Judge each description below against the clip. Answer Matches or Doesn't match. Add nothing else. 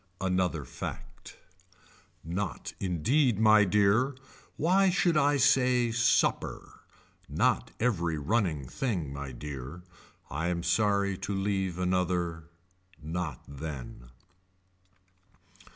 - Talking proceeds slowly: Matches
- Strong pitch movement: Matches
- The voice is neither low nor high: Doesn't match